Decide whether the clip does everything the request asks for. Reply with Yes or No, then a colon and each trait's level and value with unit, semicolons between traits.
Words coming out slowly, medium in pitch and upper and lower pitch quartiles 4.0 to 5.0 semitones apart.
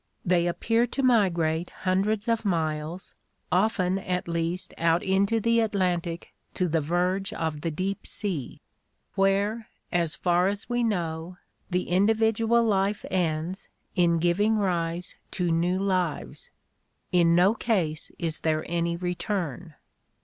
No: slow, 130 wpm; medium, 180 Hz; average, 3.1 semitones